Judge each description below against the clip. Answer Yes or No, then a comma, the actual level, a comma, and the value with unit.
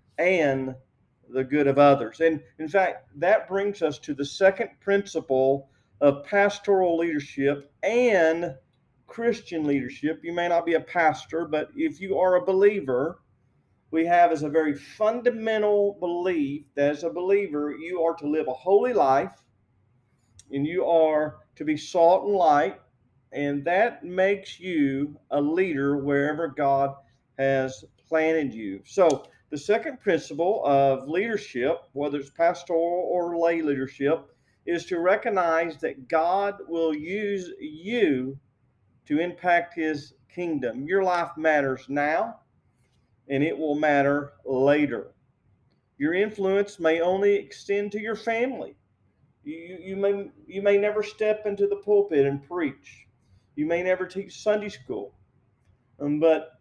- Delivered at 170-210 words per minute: No, average, 140 wpm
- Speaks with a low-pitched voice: No, medium, 160 Hz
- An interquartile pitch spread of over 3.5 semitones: Yes, wide, 5.6 semitones